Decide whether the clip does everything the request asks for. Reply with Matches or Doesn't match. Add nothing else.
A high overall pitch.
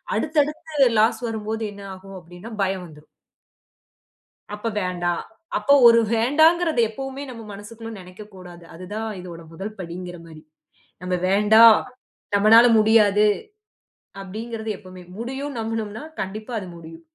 Matches